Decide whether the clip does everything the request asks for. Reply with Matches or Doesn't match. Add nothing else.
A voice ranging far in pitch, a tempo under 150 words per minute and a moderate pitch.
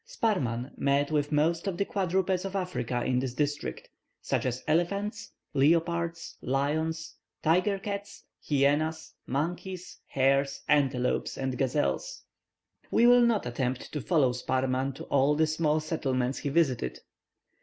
Doesn't match